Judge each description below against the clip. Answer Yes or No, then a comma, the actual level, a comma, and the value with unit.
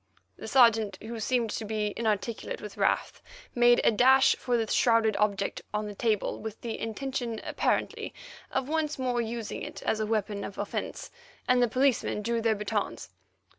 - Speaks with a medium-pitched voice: No, high, 225 Hz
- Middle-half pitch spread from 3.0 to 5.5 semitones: No, narrow, 2.5 semitones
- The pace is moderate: Yes, average, 170 wpm